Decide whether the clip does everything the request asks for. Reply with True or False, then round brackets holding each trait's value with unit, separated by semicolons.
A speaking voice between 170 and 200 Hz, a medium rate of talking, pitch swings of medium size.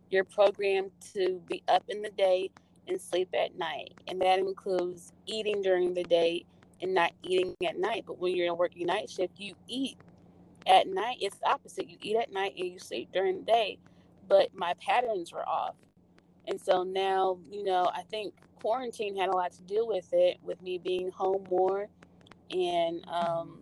True (190 Hz; 195 wpm; 4.3 semitones)